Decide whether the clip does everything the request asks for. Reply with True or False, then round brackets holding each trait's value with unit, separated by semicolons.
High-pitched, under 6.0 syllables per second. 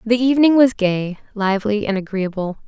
True (215 Hz; 5.4 syllables/s)